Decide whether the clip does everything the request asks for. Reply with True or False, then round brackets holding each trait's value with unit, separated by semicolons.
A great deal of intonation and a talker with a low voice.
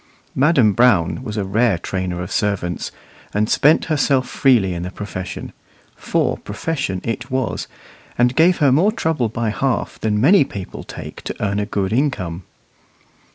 True (6.0 semitones; 110 Hz)